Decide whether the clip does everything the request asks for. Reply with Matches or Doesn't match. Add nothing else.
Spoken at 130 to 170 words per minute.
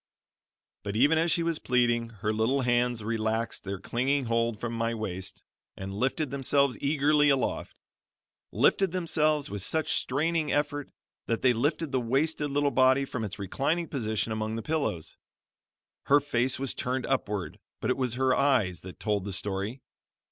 Matches